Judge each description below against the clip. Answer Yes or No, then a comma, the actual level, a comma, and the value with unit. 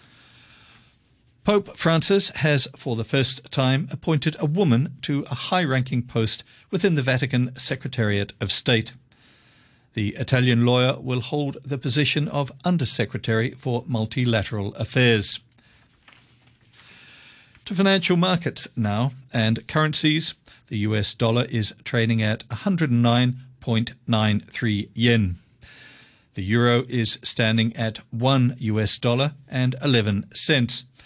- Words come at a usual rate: No, slow, 110 wpm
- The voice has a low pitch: Yes, low, 125 Hz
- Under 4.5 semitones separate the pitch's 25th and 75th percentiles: Yes, average, 3.3 semitones